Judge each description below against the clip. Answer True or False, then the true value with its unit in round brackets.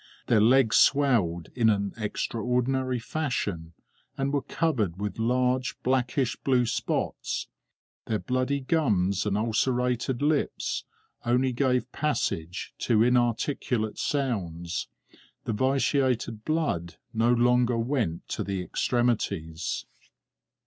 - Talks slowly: True (105 wpm)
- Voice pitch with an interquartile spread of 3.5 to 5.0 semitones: True (3.8 semitones)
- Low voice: True (120 Hz)